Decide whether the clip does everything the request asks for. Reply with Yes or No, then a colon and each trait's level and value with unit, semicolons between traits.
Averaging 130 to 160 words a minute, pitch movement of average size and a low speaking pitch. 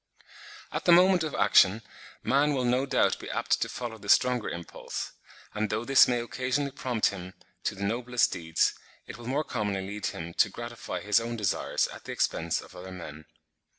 No: average, 190 wpm; average, 4.6 semitones; low, 115 Hz